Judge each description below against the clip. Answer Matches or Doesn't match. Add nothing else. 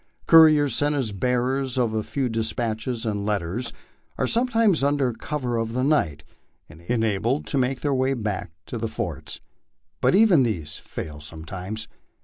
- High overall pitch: Doesn't match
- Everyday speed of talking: Matches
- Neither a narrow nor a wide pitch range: Matches